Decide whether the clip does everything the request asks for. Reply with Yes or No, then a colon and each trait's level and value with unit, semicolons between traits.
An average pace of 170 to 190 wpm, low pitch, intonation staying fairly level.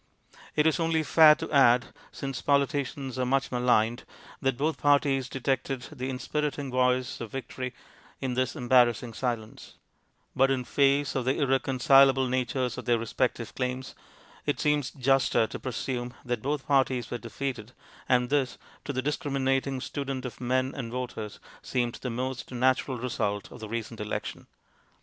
No: average, 155 wpm; low, 130 Hz; narrow, 1.9 semitones